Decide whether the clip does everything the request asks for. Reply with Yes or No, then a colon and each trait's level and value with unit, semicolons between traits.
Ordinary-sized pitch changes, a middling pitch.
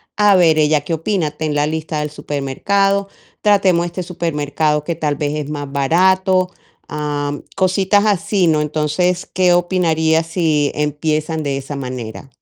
Yes: average, 3.6 semitones; medium, 160 Hz